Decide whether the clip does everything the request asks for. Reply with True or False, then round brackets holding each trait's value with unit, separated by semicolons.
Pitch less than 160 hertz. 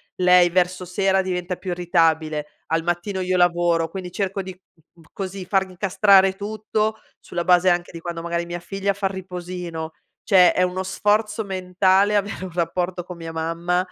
False (180 Hz)